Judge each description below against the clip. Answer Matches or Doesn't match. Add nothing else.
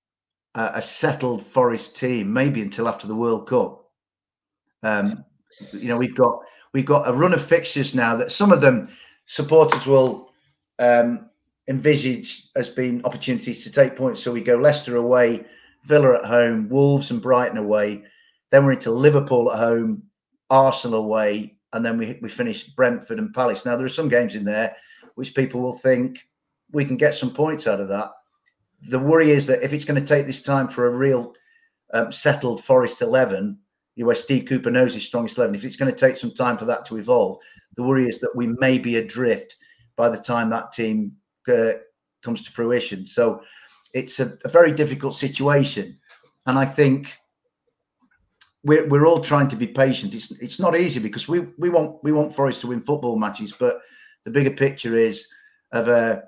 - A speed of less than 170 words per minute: Doesn't match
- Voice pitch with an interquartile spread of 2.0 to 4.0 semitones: Doesn't match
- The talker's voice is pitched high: Doesn't match